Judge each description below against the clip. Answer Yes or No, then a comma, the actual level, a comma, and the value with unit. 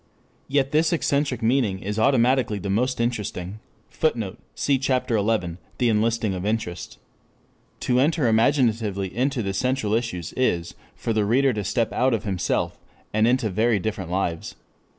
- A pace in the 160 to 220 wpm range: No, average, 150 wpm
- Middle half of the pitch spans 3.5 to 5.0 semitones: Yes, average, 4.1 semitones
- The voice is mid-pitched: No, low, 115 Hz